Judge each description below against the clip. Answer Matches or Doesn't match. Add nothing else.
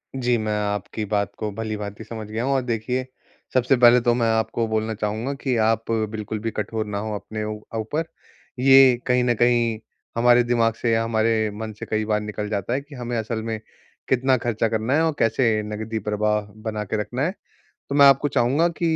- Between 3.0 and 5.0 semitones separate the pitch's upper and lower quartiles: Doesn't match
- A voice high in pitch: Doesn't match